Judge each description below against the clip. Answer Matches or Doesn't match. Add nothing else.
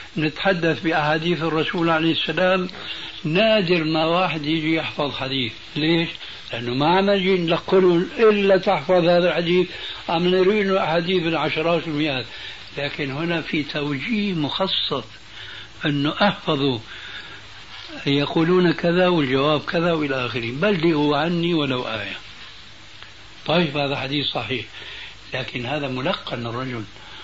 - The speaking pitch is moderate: Matches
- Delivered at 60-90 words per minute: Doesn't match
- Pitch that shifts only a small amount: Doesn't match